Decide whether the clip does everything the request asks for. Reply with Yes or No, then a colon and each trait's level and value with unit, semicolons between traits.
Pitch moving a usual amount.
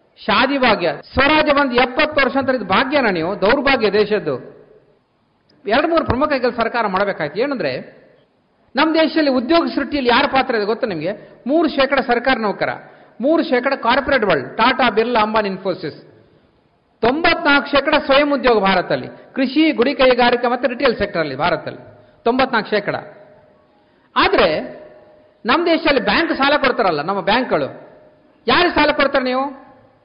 Yes: average, 4.3 semitones